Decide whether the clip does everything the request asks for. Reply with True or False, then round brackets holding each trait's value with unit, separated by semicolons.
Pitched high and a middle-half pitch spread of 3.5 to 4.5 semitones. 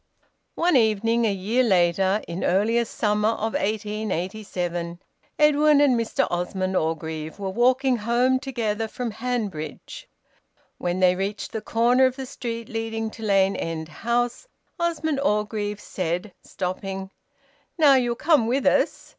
True (220 Hz; 4.2 semitones)